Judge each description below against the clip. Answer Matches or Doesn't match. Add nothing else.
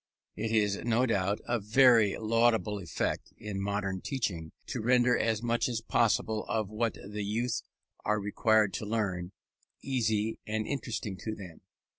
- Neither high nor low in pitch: Doesn't match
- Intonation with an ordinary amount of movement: Doesn't match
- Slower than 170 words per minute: Matches